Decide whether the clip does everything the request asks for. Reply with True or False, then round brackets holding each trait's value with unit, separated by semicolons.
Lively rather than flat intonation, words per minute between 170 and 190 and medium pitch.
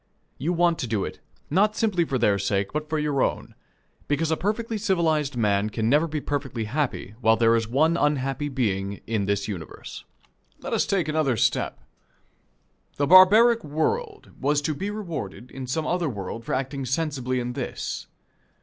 True (6.2 semitones; 175 wpm; 145 Hz)